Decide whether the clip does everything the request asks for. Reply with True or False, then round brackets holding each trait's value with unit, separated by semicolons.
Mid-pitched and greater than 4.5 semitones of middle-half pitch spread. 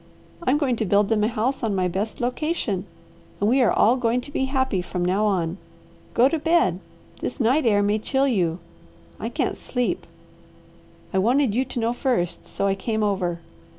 False (225 Hz; 5.0 semitones)